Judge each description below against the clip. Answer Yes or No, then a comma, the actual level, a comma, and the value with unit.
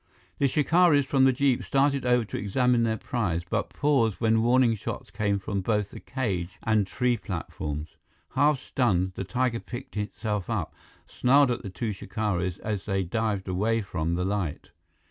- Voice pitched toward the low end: Yes, low, 110 Hz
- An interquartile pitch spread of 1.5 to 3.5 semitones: No, average, 4.6 semitones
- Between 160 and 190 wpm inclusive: Yes, average, 175 wpm